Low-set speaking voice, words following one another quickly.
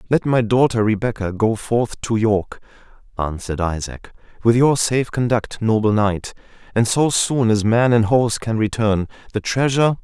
No: low, 115 Hz; average, 160 wpm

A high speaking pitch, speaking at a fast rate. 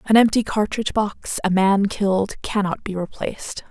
No: high, 205 Hz; average, 160 wpm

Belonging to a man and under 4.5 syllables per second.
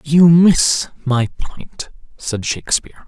Yes: male; 3.8 syllables/s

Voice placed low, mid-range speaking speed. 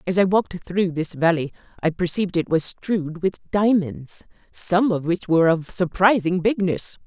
No: medium, 180 Hz; average, 170 wpm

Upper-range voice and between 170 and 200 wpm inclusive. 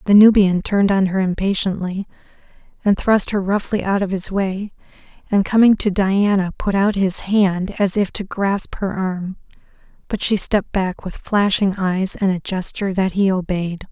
Yes: high, 195 Hz; average, 175 wpm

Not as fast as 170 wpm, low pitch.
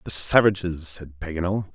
Yes: average, 140 wpm; very low, 90 Hz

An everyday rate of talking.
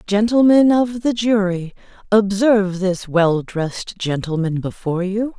No: slow, 125 wpm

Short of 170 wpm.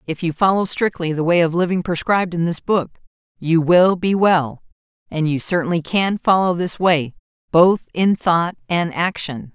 No: average, 175 wpm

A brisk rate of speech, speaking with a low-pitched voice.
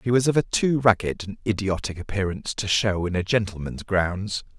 No: average, 195 wpm; low, 100 Hz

